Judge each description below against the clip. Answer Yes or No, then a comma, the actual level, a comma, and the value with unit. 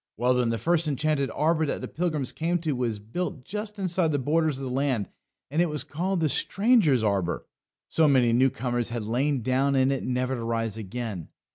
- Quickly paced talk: Yes, fast, 210 wpm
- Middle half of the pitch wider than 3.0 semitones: Yes, average, 4.7 semitones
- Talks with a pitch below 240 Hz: Yes, low, 135 Hz